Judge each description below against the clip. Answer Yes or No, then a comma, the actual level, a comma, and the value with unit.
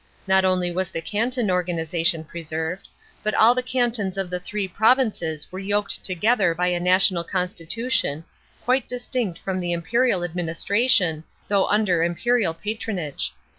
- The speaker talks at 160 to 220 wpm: No, average, 140 wpm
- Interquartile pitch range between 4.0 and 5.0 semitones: Yes, average, 4.3 semitones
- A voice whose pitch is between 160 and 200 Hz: Yes, medium, 185 Hz